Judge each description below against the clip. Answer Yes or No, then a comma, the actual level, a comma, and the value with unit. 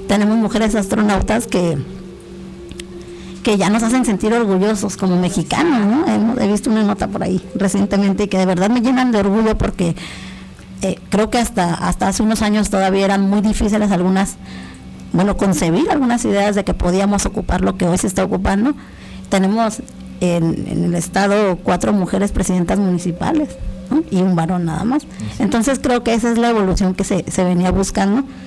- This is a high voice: Yes, high, 195 Hz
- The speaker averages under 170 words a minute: No, average, 175 wpm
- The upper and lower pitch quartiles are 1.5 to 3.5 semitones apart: Yes, average, 3.2 semitones